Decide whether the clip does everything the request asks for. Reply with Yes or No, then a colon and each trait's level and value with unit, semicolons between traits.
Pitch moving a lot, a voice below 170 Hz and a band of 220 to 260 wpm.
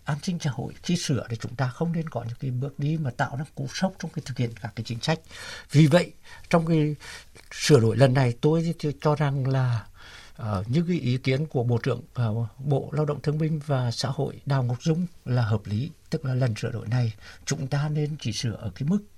No: average, 4.5 semitones; medium, 140 Hz; average, 245 wpm